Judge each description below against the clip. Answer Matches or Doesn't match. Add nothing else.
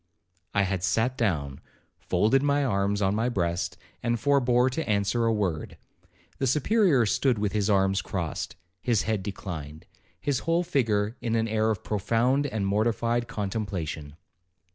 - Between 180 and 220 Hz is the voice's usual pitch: Doesn't match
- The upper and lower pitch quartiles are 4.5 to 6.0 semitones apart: Doesn't match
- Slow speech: Doesn't match